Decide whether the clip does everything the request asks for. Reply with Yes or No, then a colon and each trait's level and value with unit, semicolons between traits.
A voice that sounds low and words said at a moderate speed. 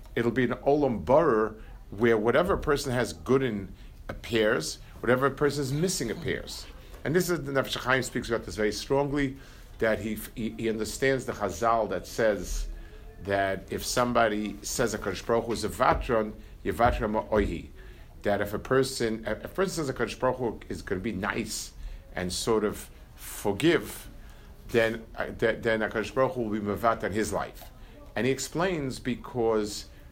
Yes: low, 115 Hz; average, 160 wpm